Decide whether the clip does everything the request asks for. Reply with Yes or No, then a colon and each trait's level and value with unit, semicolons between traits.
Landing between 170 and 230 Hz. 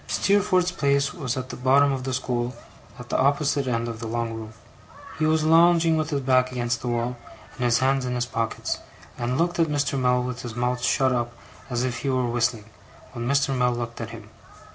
No: low, 125 Hz